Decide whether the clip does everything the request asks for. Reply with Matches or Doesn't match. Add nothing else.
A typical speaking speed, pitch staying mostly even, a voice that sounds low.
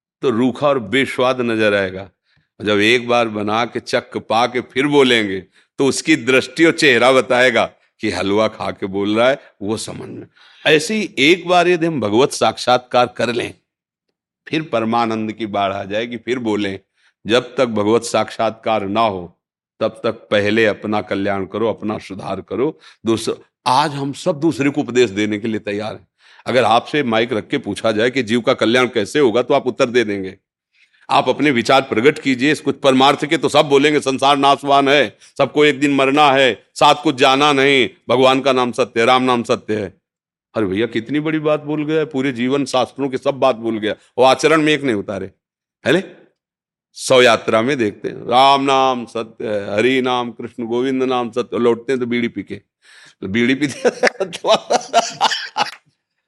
Doesn't match